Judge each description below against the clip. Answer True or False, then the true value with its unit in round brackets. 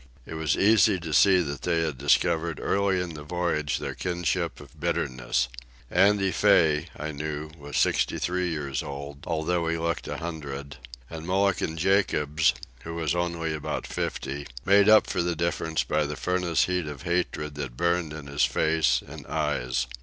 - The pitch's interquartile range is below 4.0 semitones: True (3.1 semitones)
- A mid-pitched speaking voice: False (80 Hz)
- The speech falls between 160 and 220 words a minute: True (170 wpm)